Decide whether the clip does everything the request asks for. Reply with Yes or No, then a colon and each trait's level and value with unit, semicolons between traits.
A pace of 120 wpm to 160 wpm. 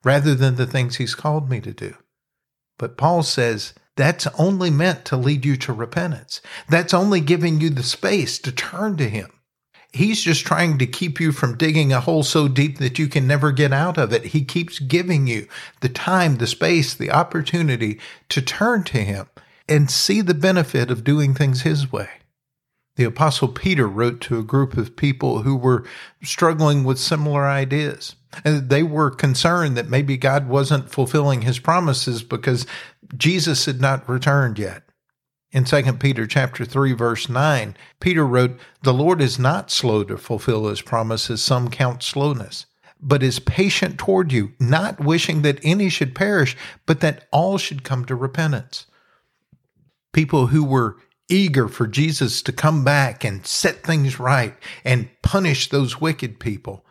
No: average, 170 wpm